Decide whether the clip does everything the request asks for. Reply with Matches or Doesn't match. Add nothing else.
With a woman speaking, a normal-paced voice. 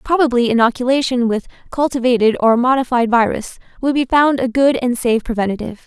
Matches